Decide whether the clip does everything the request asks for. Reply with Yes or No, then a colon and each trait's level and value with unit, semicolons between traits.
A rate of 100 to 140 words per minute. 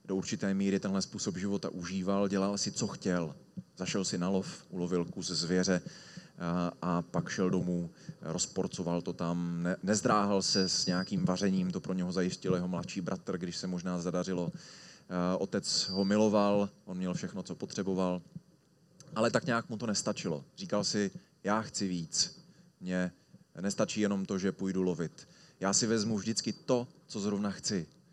No: average, 160 wpm